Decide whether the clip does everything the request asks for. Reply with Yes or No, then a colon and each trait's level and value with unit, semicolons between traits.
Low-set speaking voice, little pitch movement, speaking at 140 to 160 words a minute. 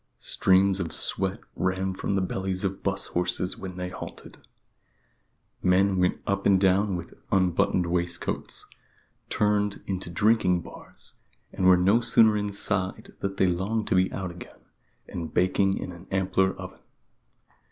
Yes: very low, 95 Hz; narrow, 1.4 semitones; average, 145 wpm